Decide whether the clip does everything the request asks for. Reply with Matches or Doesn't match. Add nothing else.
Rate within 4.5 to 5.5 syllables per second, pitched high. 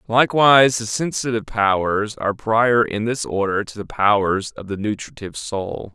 Doesn't match